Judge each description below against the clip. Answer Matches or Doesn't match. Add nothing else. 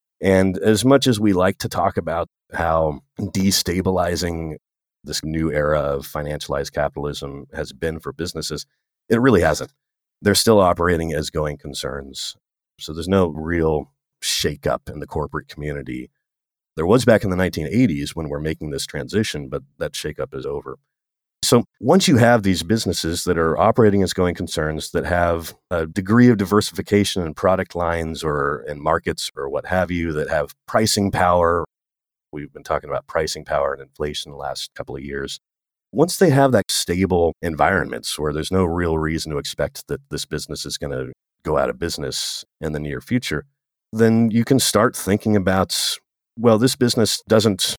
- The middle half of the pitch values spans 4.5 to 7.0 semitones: Matches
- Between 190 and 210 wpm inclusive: Doesn't match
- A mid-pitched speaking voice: Doesn't match